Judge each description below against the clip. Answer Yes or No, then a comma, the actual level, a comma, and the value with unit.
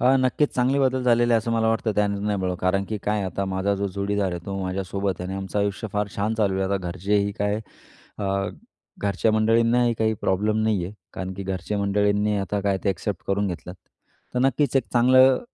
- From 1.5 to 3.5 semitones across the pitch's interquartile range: Yes, narrow, 2.5 semitones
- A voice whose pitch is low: Yes, low, 100 Hz